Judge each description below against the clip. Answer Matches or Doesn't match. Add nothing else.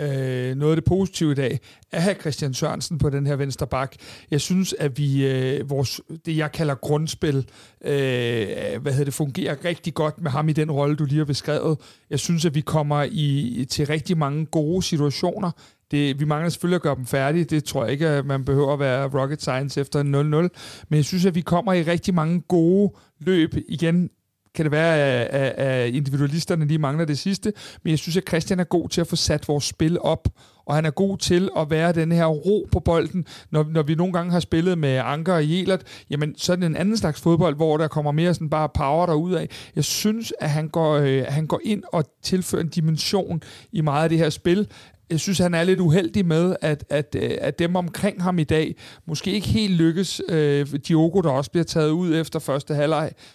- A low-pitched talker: Doesn't match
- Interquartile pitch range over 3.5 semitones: Doesn't match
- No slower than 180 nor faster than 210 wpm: Doesn't match